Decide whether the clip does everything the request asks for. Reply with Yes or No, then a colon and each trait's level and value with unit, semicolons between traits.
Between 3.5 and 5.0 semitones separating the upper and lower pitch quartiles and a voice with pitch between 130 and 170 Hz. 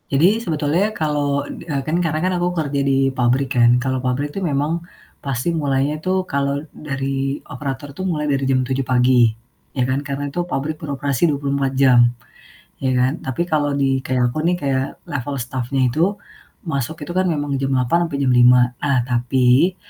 No: average, 2.8 semitones; medium, 140 Hz